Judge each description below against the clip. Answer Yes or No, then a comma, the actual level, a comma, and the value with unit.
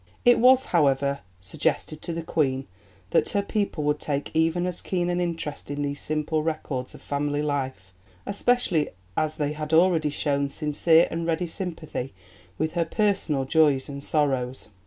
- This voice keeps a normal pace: Yes, average, 160 wpm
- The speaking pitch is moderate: Yes, medium, 155 Hz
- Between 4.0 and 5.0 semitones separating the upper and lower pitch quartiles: No, average, 3.1 semitones